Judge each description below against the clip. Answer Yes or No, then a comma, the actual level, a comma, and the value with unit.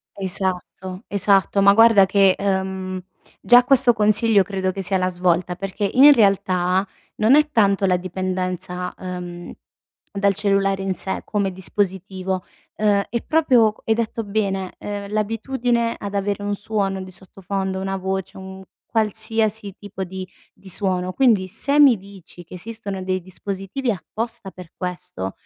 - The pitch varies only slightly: Yes, narrow, 2.3 semitones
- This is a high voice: Yes, high, 195 Hz